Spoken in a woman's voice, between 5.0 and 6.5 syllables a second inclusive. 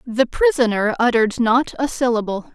Yes: female; 5.1 syllables/s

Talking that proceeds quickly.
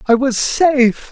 No: average, 160 wpm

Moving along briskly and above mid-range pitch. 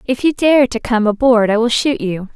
Yes: fast, 255 wpm; high, 240 Hz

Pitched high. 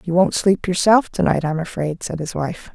No: medium, 175 Hz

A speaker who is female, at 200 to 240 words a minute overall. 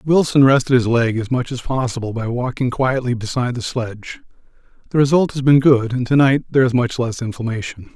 No: male; fast, 205 wpm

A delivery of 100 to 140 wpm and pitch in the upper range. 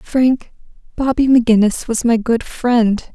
Yes: slow, 135 wpm; high, 235 Hz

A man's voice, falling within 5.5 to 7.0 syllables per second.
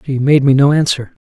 Yes: male; 5.7 syllables/s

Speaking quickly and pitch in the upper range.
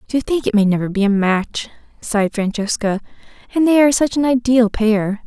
No: average, 195 wpm; high, 225 Hz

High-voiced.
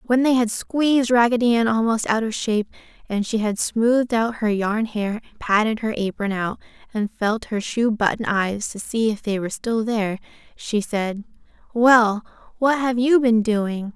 Yes: high, 225 Hz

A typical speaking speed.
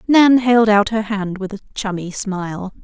Yes: average, 190 wpm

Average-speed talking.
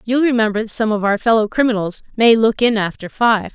No: fast, 220 wpm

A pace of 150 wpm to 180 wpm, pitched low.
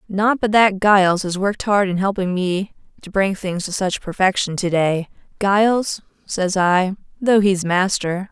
No: average, 175 wpm; high, 190 Hz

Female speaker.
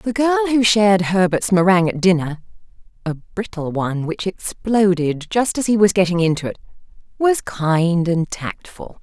Yes: female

